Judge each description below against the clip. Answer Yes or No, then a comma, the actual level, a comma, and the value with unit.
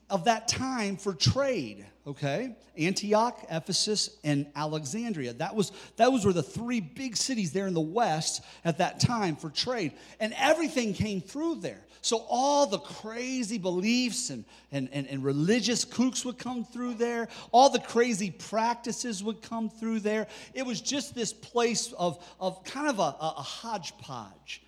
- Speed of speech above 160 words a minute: Yes, average, 170 wpm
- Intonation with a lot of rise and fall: Yes, wide, 6.1 semitones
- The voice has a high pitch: Yes, high, 215 Hz